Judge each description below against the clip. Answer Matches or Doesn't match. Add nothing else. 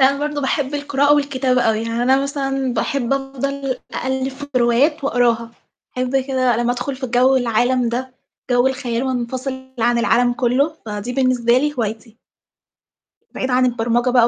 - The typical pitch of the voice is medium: Doesn't match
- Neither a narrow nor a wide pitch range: Doesn't match